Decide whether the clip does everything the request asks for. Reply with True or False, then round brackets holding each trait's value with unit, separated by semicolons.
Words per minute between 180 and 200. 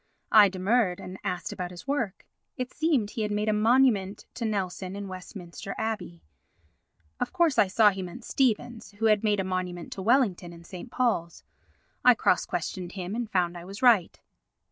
True (185 wpm)